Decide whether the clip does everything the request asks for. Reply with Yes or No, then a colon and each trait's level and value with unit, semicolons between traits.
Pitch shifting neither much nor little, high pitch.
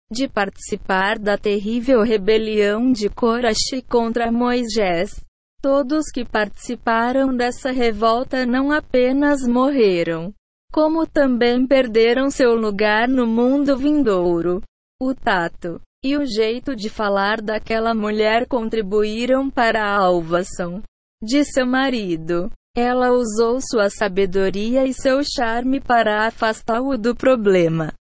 Yes: average, 3.6 semitones; high, 230 Hz